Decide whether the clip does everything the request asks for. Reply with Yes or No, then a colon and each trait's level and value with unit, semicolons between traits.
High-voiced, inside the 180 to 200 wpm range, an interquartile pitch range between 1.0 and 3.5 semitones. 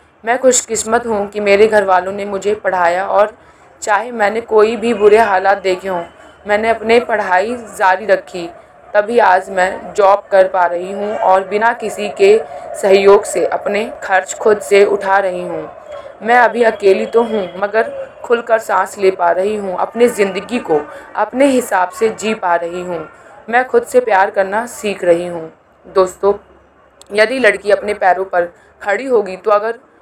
No: high, 205 Hz; average, 170 wpm; average, 3.1 semitones